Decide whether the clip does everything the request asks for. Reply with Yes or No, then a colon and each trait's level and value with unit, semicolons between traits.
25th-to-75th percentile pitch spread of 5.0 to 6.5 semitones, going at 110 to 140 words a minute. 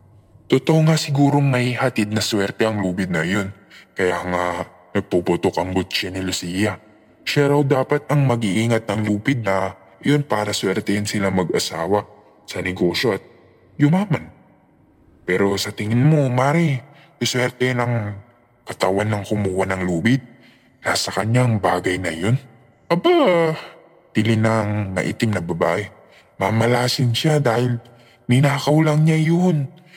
Yes: wide, 5.5 semitones; slow, 135 wpm